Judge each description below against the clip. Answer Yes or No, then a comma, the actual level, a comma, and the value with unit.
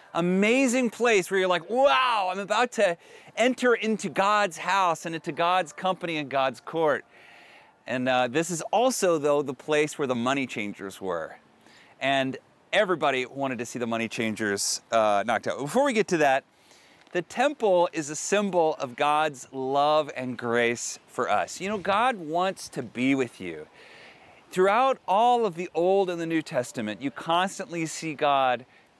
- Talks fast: No, average, 170 wpm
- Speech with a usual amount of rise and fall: No, wide, 6.5 semitones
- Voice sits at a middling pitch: Yes, medium, 165 Hz